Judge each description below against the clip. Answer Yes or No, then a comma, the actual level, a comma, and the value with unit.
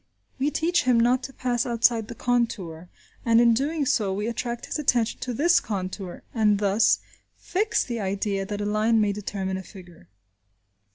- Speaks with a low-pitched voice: No, high, 225 Hz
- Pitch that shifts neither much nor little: Yes, average, 3.7 semitones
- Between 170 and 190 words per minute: Yes, average, 175 wpm